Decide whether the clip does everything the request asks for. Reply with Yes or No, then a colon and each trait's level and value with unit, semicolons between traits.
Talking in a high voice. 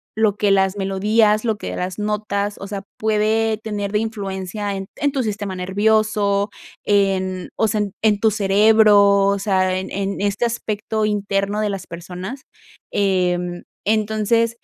Yes: high, 205 Hz